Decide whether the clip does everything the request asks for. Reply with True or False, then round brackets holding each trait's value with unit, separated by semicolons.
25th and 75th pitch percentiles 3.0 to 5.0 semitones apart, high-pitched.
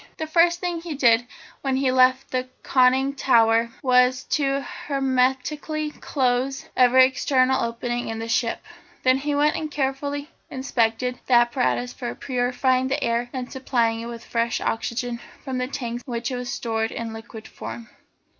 False (2.4 semitones; 255 Hz)